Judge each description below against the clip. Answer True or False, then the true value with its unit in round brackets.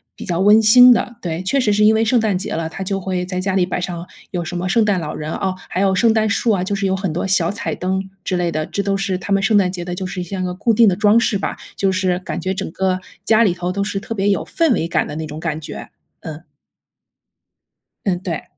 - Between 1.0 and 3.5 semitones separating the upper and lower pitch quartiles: True (2.6 semitones)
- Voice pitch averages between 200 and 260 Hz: False (190 Hz)